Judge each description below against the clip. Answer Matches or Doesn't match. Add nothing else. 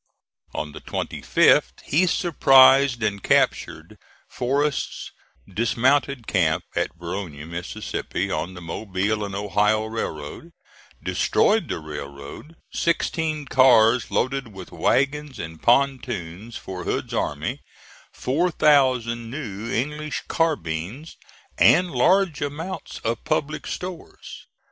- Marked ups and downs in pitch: Matches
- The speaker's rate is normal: Doesn't match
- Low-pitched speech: Matches